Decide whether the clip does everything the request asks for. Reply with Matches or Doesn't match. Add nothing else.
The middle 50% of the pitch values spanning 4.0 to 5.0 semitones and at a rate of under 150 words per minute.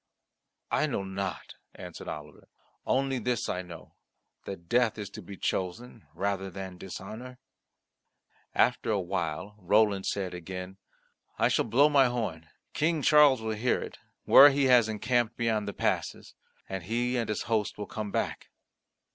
Doesn't match